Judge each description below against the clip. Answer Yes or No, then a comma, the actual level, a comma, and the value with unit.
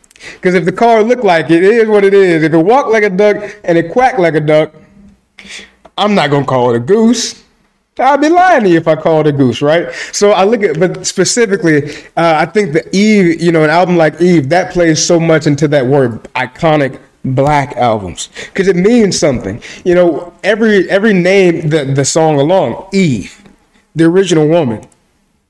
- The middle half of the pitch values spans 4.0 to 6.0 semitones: Yes, average, 4.7 semitones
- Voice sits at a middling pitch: Yes, medium, 175 Hz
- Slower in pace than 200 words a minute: No, fast, 205 wpm